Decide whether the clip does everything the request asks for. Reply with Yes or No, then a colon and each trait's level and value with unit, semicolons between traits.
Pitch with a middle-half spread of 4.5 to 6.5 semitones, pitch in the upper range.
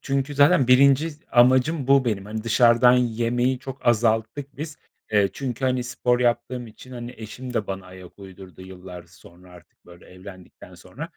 No: average, 4.8 semitones; low, 120 Hz